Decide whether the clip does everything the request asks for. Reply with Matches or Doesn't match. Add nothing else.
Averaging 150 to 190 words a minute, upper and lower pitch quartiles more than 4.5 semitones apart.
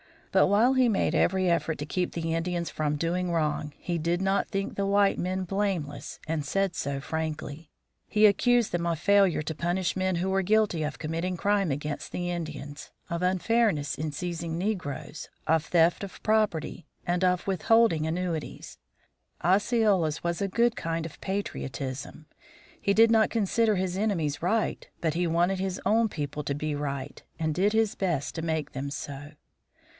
Doesn't match